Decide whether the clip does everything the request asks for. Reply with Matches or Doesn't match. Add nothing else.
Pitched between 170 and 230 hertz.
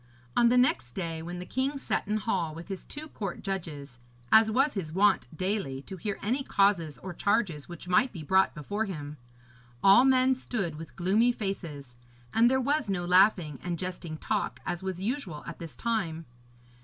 Matches